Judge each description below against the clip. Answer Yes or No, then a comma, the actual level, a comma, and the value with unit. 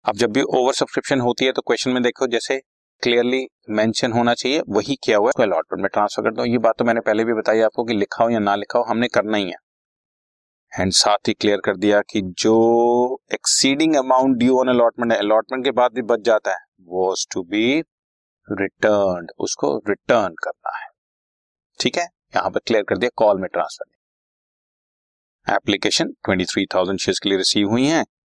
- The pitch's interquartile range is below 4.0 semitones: Yes, average, 3.5 semitones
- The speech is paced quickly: Yes, fast, 195 wpm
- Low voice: Yes, low, 115 Hz